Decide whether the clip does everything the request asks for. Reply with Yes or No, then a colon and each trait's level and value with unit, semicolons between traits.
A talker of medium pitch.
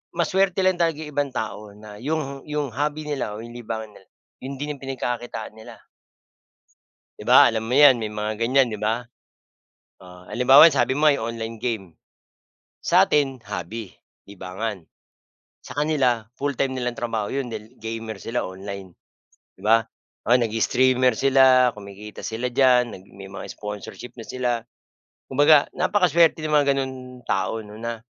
No: low, 120 Hz